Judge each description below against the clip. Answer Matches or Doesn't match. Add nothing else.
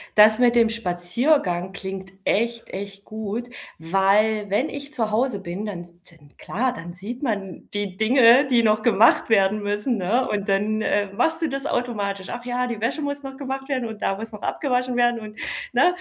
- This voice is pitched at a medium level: Doesn't match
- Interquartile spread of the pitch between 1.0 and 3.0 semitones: Doesn't match